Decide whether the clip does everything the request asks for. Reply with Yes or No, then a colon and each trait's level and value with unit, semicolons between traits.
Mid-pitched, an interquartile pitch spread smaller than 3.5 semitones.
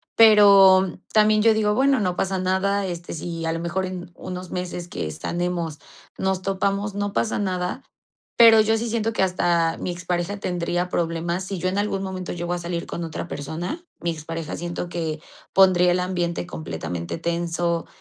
Yes: medium, 180 Hz; narrow, 2.5 semitones